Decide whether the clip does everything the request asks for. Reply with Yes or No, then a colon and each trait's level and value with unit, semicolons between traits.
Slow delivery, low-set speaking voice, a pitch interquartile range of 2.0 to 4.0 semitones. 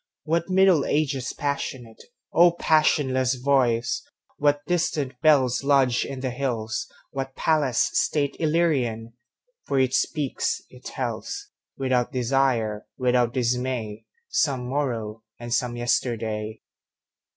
Yes: slow, 95 wpm; low, 130 Hz; average, 3.3 semitones